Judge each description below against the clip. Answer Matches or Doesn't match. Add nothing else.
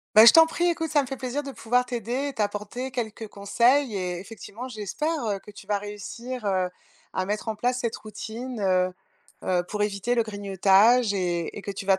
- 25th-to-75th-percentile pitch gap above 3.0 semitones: Matches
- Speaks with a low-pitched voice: Doesn't match